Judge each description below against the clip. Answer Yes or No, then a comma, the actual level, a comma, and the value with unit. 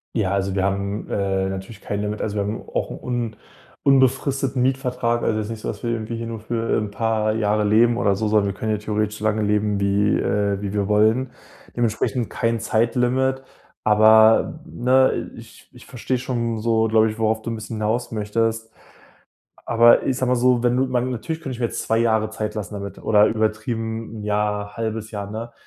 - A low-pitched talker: Yes, low, 110 Hz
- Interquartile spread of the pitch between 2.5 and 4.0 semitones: No, narrow, 2.0 semitones